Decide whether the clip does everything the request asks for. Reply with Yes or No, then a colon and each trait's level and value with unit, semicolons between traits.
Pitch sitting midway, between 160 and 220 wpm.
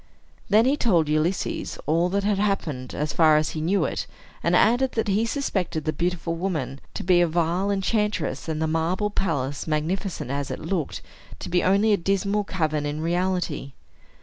Yes: medium, 175 Hz; average, 180 wpm